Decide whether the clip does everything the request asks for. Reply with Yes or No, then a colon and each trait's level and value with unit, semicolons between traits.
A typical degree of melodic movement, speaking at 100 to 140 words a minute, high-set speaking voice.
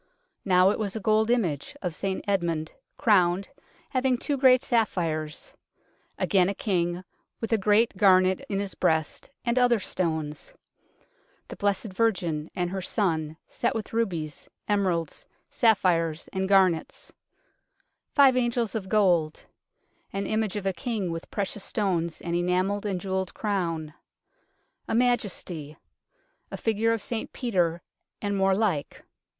Yes: average, 4.1 semitones; slow, 135 wpm; high, 195 Hz